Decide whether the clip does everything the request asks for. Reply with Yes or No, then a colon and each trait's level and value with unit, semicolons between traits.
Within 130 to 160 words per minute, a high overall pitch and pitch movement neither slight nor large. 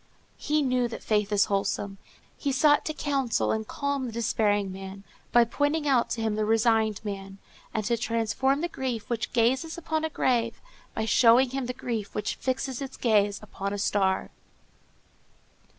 No: average, 170 wpm; high, 230 Hz; average, 4.1 semitones